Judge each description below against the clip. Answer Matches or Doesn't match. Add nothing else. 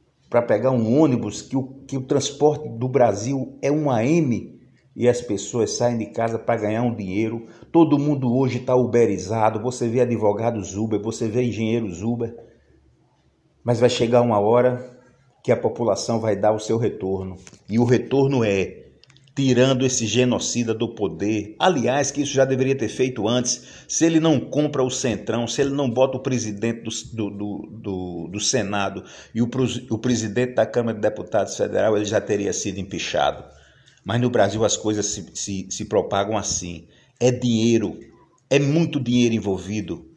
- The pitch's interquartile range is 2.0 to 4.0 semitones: Matches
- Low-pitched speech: Matches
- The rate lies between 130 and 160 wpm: Doesn't match